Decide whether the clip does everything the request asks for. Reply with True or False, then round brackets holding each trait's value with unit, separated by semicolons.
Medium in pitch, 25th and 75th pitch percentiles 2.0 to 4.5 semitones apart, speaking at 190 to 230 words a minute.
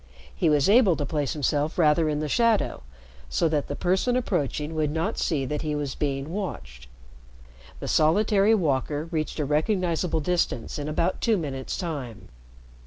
False (155 Hz; 3.7 semitones; 165 wpm)